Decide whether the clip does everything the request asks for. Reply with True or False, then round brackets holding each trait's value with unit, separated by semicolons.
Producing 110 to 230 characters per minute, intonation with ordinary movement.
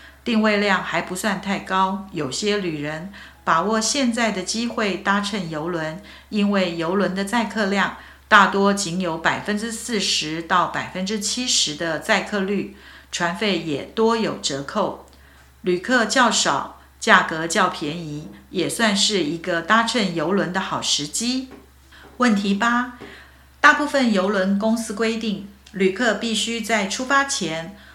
True (215 characters per minute; 4.3 semitones)